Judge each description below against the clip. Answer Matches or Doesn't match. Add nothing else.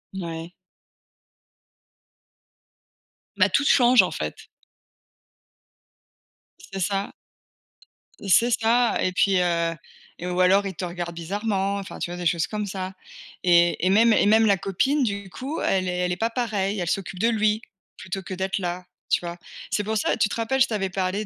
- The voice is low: Doesn't match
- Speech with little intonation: Doesn't match